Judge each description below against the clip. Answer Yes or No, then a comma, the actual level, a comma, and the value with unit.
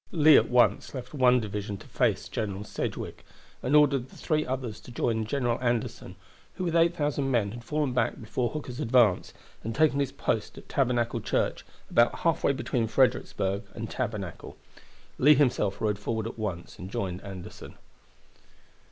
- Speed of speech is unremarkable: Yes, average, 160 wpm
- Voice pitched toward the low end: Yes, low, 120 Hz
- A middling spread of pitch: Yes, average, 4.6 semitones